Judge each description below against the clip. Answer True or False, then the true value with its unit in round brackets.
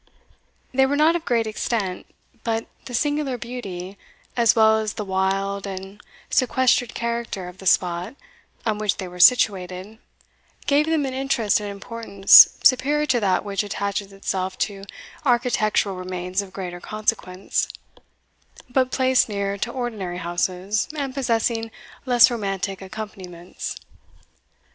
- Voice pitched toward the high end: True (210 Hz)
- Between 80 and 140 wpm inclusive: True (135 wpm)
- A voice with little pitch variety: False (4.2 semitones)